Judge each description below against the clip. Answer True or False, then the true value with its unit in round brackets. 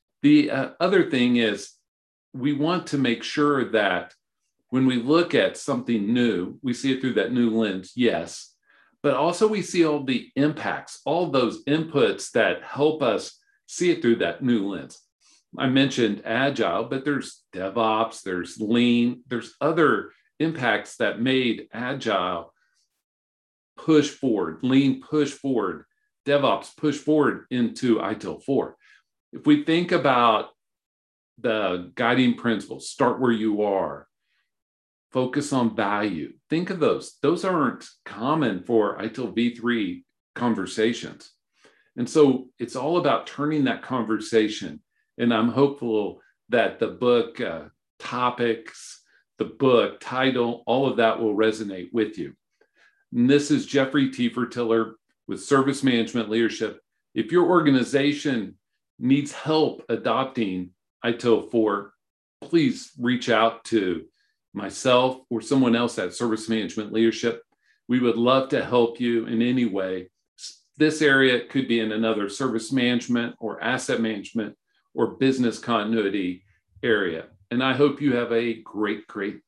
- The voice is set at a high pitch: False (120 Hz)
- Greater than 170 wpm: False (135 wpm)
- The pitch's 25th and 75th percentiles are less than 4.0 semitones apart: True (3.5 semitones)